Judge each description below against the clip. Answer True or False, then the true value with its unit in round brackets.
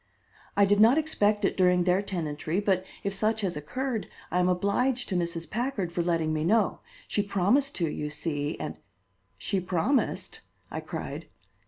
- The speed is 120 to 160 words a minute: False (175 wpm)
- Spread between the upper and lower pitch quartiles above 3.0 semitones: True (4.0 semitones)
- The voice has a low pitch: False (190 Hz)